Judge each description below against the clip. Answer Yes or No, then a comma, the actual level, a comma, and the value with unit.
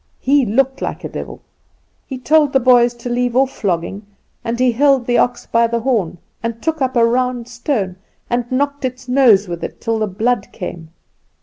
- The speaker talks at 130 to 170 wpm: No, average, 195 wpm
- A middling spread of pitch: No, narrow, 2.3 semitones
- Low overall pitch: No, high, 245 Hz